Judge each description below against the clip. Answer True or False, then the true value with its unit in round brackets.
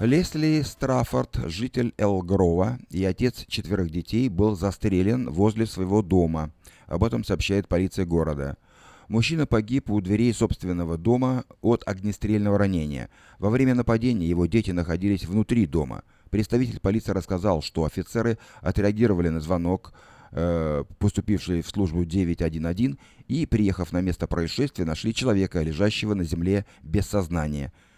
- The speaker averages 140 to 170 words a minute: False (125 wpm)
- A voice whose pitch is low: True (100 Hz)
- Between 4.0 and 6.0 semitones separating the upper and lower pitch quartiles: True (4.5 semitones)